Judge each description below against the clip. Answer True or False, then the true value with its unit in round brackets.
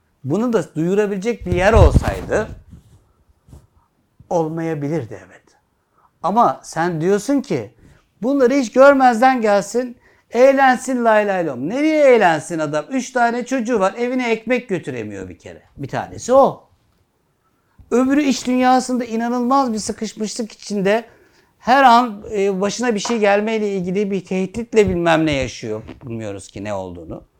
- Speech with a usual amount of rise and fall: False (6.4 semitones)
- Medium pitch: False (220 Hz)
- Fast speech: False (125 wpm)